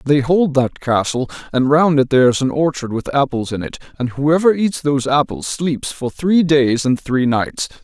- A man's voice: Yes, male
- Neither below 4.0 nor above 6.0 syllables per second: Yes, 4.8 syllables/s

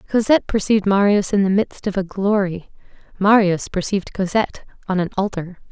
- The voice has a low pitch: No, high, 195 Hz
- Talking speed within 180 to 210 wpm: No, average, 155 wpm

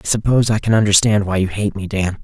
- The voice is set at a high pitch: No, low, 105 Hz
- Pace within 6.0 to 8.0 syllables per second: Yes, 6.6 syllables/s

